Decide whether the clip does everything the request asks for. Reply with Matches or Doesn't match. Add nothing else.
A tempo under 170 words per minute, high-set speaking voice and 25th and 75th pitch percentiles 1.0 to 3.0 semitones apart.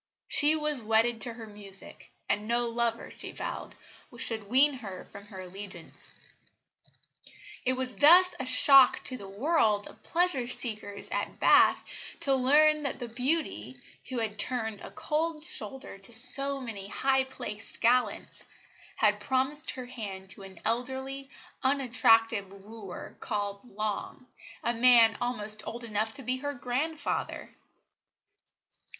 Doesn't match